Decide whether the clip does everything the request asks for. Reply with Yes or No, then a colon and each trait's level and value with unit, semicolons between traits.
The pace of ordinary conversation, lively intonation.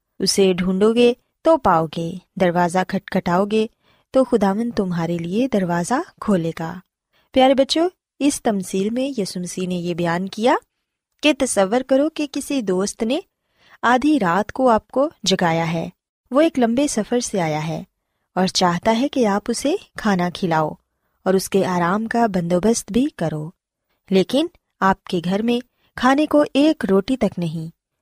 Yes: average, 160 wpm; wide, 6.1 semitones